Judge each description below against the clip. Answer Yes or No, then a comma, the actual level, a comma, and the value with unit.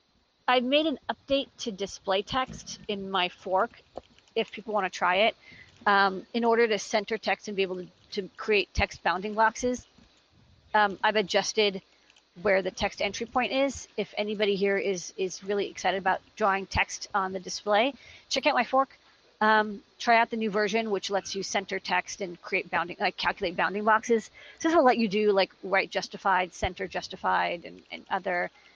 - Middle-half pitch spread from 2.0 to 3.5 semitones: Yes, average, 2.9 semitones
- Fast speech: No, average, 185 wpm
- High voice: Yes, high, 205 Hz